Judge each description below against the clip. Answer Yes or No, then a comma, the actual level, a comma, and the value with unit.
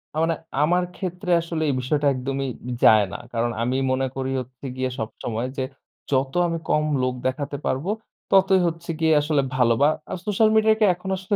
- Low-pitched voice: No, medium, 145 Hz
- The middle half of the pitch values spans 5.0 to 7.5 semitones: Yes, average, 5.3 semitones